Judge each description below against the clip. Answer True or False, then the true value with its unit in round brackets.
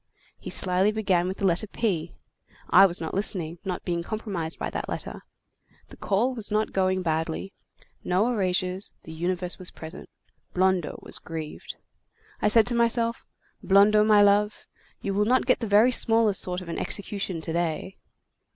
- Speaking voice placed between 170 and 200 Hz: True (190 Hz)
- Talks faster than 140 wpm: True (170 wpm)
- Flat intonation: False (3.2 semitones)